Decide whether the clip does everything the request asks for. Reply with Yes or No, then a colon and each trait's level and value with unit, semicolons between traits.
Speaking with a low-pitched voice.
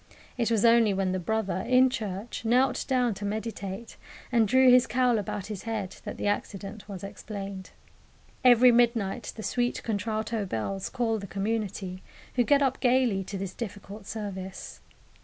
No: high, 220 Hz